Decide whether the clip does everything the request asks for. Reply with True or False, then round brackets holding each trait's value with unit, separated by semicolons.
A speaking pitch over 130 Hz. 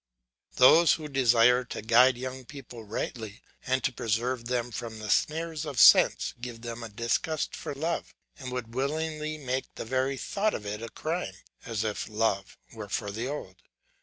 False (125 Hz)